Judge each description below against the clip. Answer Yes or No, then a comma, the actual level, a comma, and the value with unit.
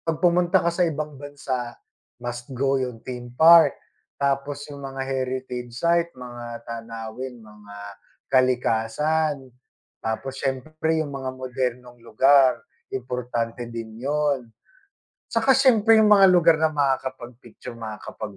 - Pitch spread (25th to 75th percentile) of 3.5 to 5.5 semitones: Yes, average, 4.1 semitones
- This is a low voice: Yes, low, 130 Hz